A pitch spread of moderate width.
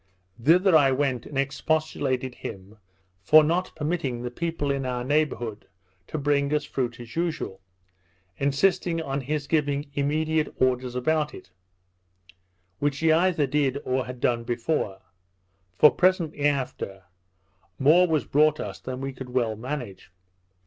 Yes: average, 3.6 semitones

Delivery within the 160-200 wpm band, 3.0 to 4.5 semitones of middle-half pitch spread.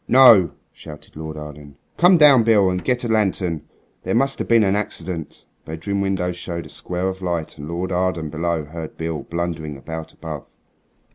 Yes: average, 185 wpm; average, 3.8 semitones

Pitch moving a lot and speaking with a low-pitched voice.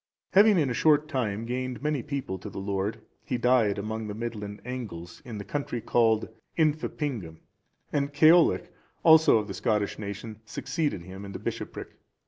Yes: wide, 5.8 semitones; low, 115 Hz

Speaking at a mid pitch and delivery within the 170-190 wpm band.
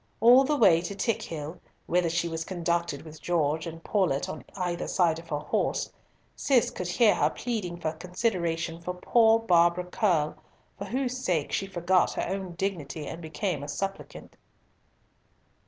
No: medium, 175 Hz; average, 160 wpm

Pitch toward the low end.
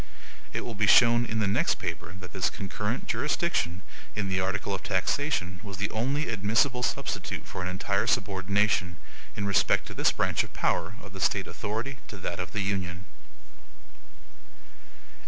Yes: low, 100 Hz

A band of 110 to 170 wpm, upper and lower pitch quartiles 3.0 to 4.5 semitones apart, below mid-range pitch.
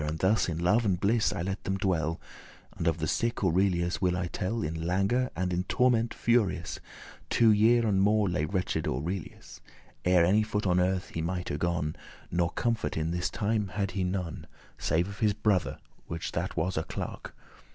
No: average, 190 wpm; average, 3.3 semitones; very low, 95 Hz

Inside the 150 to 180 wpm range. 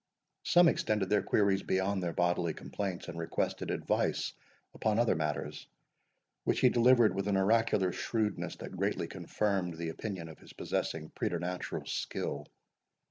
No: average, 140 wpm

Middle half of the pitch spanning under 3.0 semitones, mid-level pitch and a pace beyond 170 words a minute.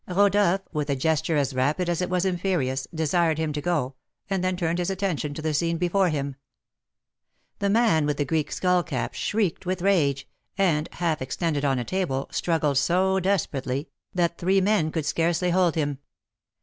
No: average, 3.9 semitones; medium, 170 Hz; average, 180 wpm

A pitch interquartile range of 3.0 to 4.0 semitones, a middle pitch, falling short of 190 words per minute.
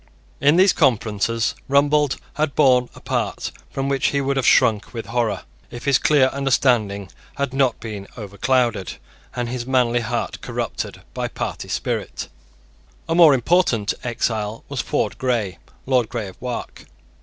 No: average, 3.7 semitones; low, 125 Hz; average, 150 wpm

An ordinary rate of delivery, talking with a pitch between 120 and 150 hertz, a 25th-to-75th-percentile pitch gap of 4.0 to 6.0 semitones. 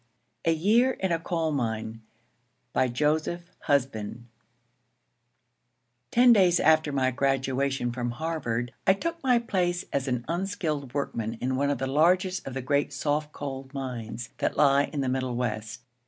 Yes: average, 155 wpm; medium, 140 Hz; average, 5.0 semitones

